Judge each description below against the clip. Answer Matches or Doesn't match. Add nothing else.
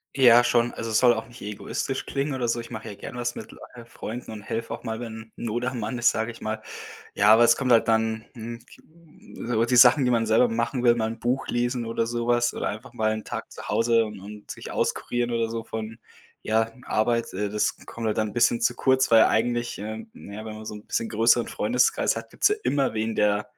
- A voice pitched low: Matches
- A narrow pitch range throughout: Matches